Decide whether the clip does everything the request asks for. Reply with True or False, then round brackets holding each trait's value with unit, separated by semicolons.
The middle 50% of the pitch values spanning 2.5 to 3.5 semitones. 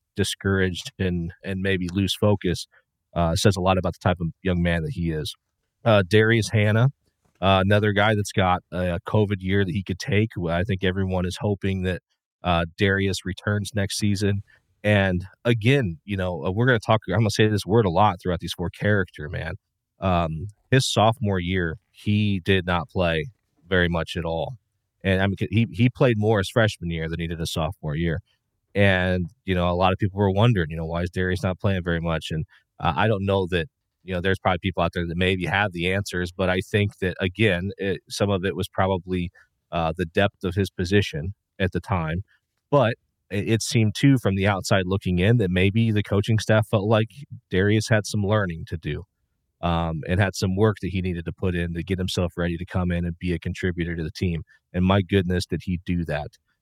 True (2.8 semitones)